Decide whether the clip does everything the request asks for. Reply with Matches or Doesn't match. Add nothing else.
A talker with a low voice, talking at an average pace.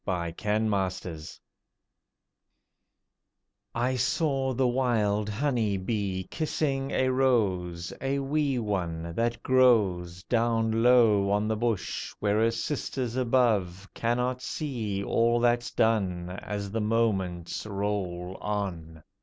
Doesn't match